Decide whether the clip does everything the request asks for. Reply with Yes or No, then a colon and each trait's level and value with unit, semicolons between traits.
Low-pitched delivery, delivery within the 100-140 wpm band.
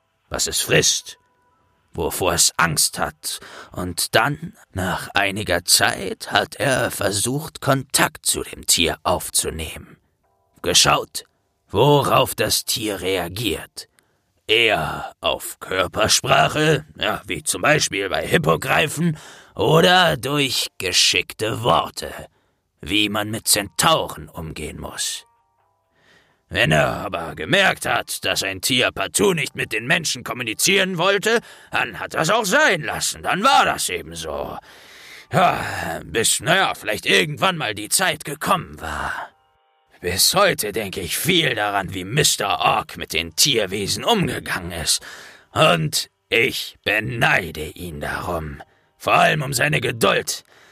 Yes: low, 115 Hz; slow, 125 wpm